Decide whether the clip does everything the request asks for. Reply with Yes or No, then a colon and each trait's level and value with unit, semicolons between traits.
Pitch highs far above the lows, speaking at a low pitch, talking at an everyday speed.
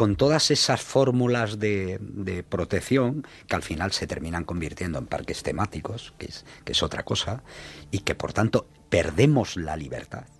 Yes: wide, 6.5 semitones; low, 100 Hz; average, 165 wpm